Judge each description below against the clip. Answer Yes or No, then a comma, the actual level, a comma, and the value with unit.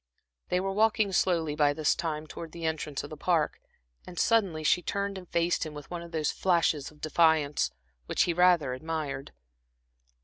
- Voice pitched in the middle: Yes, medium, 165 Hz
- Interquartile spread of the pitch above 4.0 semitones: No, average, 2.8 semitones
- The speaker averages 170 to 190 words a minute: Yes, average, 180 wpm